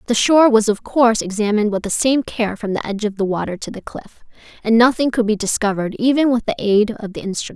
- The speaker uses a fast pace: Yes, fast, 245 wpm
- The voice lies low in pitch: No, high, 220 Hz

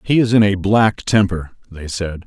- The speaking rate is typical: No, fast, 210 wpm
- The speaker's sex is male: Yes, male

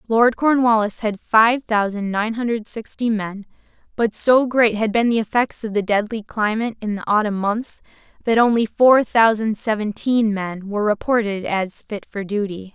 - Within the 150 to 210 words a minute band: Yes, average, 170 wpm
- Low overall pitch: No, high, 220 Hz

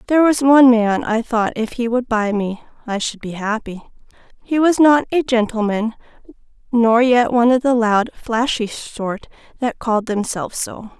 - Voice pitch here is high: Yes, high, 235 Hz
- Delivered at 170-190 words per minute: Yes, average, 175 wpm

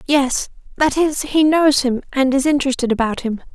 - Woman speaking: Yes, female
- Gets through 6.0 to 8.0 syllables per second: No, 5.1 syllables/s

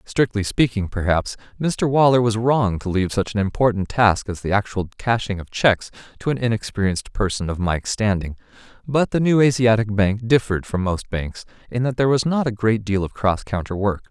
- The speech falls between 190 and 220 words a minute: Yes, average, 200 wpm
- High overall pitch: No, low, 110 Hz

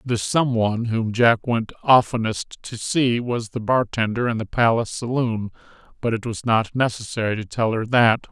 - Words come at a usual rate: Yes, average, 180 wpm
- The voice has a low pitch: Yes, low, 115 Hz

